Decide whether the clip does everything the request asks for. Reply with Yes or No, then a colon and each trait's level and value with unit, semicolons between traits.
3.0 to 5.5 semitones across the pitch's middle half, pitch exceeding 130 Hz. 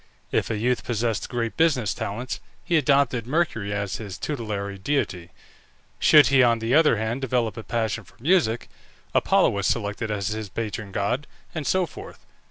No: average, 4.6 semitones; low, 115 Hz